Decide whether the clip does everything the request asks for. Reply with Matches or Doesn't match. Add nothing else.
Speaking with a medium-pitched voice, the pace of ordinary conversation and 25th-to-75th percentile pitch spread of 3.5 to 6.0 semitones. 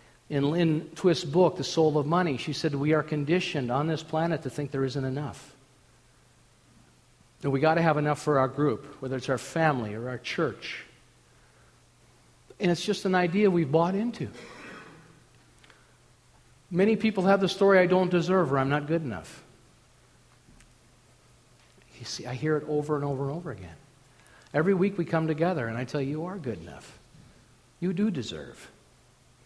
Matches